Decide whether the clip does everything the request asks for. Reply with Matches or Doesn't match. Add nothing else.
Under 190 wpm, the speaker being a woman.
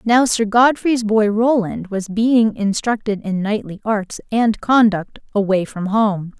Matches